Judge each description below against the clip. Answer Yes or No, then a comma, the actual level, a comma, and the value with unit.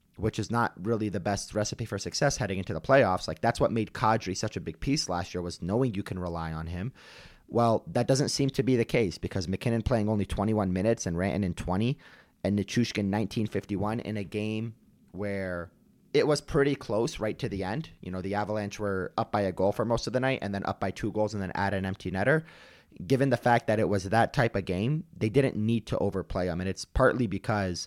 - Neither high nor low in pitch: No, low, 105 Hz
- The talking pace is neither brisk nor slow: No, fast, 235 wpm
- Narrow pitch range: No, average, 3.4 semitones